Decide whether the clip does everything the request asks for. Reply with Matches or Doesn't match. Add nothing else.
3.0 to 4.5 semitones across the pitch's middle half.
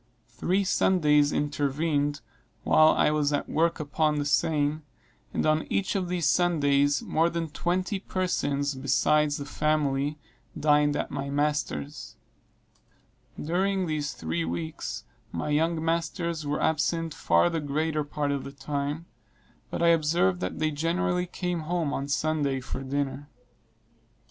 Doesn't match